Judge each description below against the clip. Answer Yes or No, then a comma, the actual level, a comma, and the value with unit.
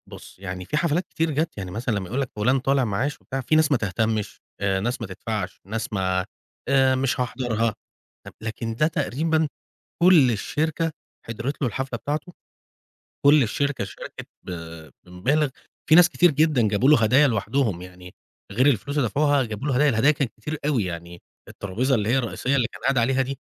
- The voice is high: No, low, 125 Hz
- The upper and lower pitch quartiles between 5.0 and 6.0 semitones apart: Yes, average, 5.3 semitones